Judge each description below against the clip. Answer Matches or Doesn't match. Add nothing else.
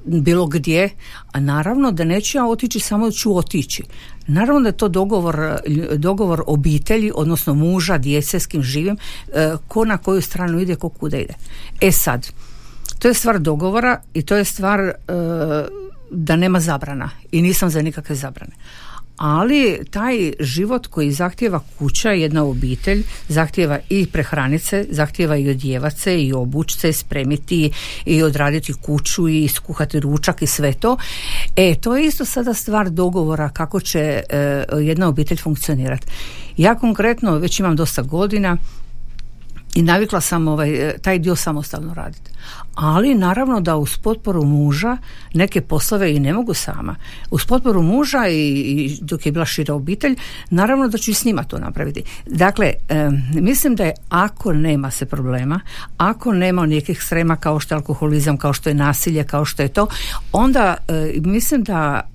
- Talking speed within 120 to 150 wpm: Doesn't match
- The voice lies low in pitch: Doesn't match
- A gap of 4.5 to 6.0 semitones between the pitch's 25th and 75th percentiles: Matches